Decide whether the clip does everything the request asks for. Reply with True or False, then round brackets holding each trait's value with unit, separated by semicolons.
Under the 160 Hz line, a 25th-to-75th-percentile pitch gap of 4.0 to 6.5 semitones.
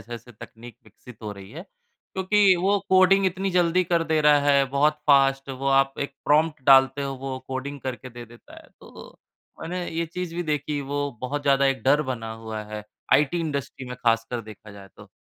True (140 Hz; 4.6 semitones)